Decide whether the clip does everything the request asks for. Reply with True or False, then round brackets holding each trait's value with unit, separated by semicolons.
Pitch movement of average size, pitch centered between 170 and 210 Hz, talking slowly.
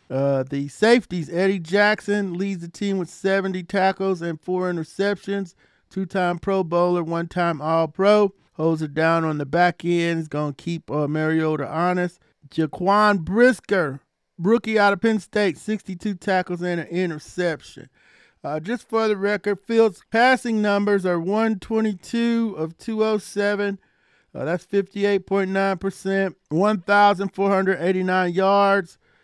True (3.3 semitones; 190 Hz; 125 wpm)